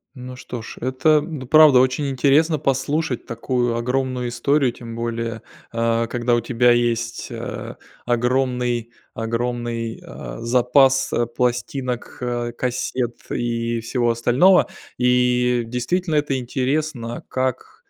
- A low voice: Yes, low, 125 Hz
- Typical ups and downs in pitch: No, narrow, 2.1 semitones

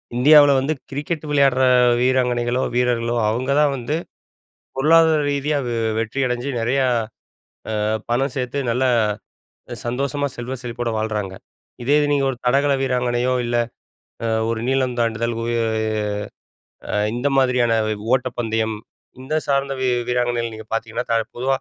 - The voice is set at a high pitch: No, low, 125 Hz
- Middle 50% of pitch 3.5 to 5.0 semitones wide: No, narrow, 2.6 semitones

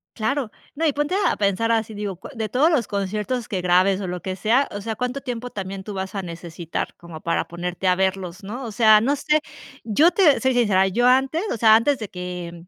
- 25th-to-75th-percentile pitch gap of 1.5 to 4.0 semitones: No, average, 5.0 semitones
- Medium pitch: No, high, 210 Hz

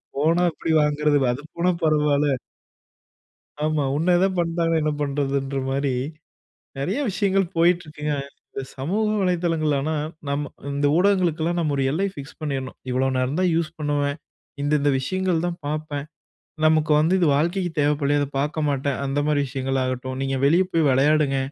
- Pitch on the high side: No, medium, 150 Hz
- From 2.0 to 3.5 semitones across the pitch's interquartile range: Yes, average, 3.1 semitones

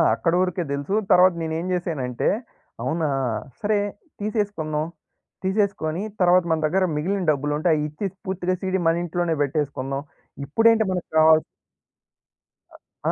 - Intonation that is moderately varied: Yes, average, 3.7 semitones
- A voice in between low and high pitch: Yes, medium, 170 Hz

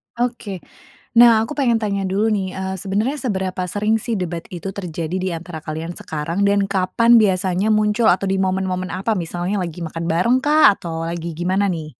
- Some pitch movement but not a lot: Yes, average, 3.4 semitones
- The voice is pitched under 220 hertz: Yes, high, 190 Hz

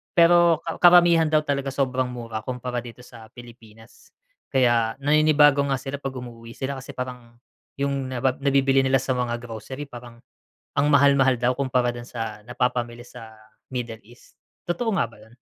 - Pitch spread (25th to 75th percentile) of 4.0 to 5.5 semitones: No, average, 2.7 semitones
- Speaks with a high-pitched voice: No, low, 125 Hz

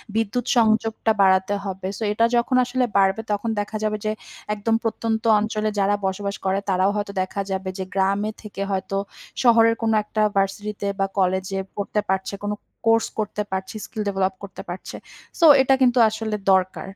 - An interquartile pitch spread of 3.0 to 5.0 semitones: No, narrow, 2.5 semitones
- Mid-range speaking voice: No, high, 205 Hz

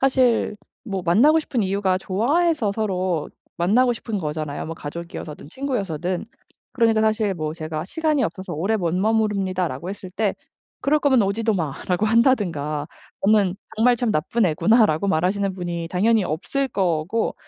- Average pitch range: Yes, average, 4.9 semitones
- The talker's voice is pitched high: Yes, high, 195 Hz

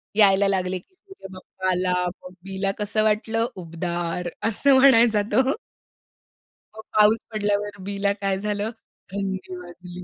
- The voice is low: No, high, 200 Hz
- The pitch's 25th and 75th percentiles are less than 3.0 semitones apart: Yes, narrow, 2.6 semitones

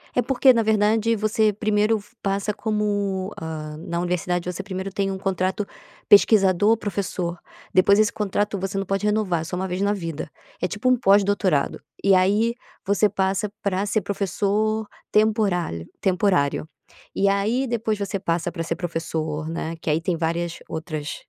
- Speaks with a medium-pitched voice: No, high, 195 Hz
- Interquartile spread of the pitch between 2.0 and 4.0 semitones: Yes, average, 3.2 semitones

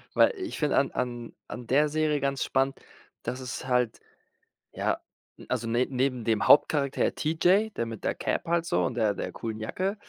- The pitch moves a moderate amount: Yes, average, 4.3 semitones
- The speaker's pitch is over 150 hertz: No, low, 135 Hz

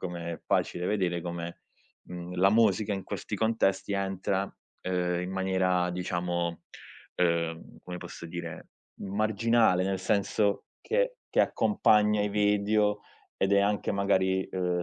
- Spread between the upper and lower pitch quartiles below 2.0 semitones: No, narrow, 2.6 semitones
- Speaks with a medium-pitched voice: No, very low, 95 Hz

